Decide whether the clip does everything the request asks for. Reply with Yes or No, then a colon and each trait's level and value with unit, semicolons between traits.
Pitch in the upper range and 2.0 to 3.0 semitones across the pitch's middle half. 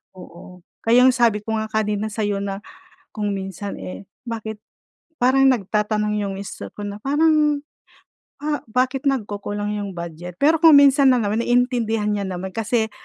No: high, 215 Hz; average, 3.8 semitones